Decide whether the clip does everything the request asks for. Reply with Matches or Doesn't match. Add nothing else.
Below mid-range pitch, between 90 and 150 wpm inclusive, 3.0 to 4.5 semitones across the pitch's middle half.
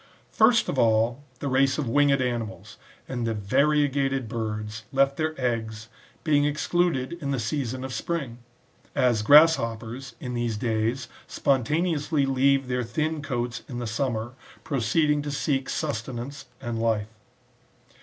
Matches